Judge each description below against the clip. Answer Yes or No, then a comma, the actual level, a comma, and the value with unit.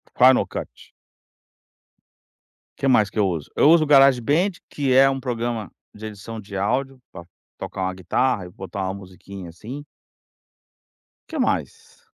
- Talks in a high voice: No, low, 110 Hz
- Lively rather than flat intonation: Yes, wide, 5.7 semitones